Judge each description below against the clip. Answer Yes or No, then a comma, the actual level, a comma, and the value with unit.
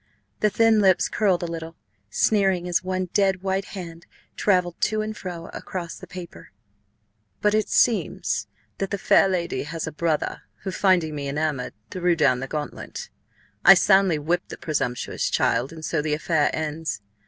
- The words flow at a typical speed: Yes, average, 170 wpm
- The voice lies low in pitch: No, medium, 175 Hz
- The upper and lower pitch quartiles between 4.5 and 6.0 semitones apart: No, average, 3.7 semitones